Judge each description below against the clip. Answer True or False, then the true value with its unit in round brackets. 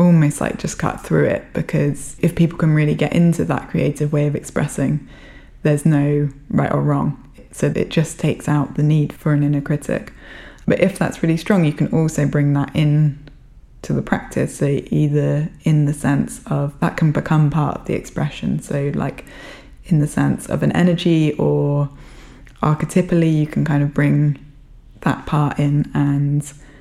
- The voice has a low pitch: False (150 Hz)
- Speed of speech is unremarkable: True (180 wpm)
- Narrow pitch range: True (1.6 semitones)